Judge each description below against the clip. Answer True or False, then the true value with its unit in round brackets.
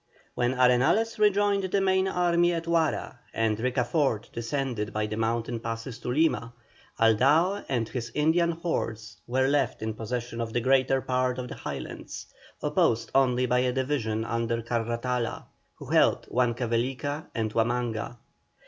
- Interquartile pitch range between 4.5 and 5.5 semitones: False (4.0 semitones)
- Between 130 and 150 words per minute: True (145 wpm)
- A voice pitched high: False (125 Hz)